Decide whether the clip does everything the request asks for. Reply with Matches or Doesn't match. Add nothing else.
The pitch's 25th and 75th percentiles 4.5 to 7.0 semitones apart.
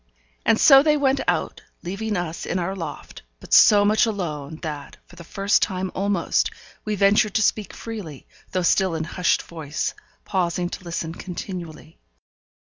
Doesn't match